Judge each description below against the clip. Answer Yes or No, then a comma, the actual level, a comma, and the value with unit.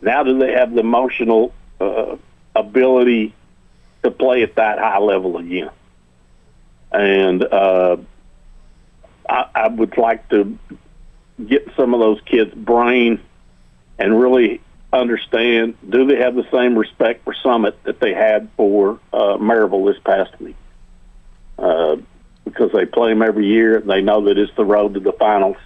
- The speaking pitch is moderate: No, low, 105 Hz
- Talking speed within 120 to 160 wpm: Yes, average, 150 wpm